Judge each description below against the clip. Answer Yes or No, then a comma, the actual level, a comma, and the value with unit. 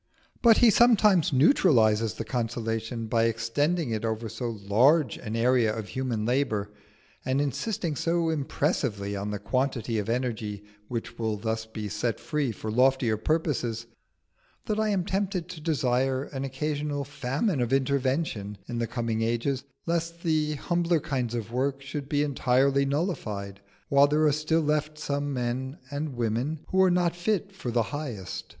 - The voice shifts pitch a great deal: No, average, 5.0 semitones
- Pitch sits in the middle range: No, low, 130 Hz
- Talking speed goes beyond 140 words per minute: Yes, average, 160 wpm